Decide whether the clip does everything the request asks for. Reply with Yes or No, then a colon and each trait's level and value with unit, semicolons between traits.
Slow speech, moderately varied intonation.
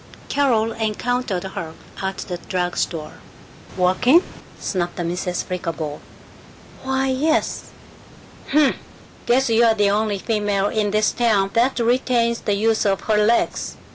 Yes: slow, 125 wpm; average, 4.0 semitones